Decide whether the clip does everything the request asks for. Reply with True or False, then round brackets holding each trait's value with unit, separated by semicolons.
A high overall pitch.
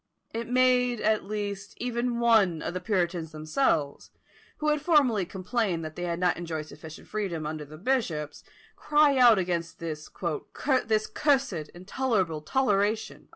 True (200 Hz)